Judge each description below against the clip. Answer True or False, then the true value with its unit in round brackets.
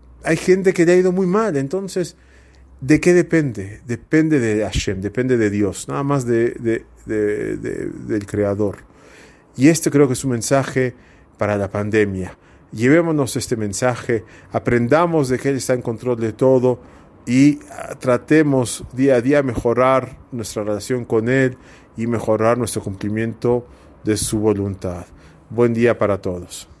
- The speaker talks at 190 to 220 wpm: False (155 wpm)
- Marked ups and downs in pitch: False (4.4 semitones)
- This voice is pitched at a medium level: False (120 Hz)